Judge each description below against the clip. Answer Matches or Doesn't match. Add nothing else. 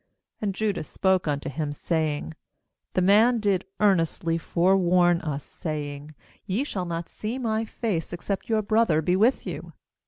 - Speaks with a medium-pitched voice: Matches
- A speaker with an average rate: Matches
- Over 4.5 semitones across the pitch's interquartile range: Matches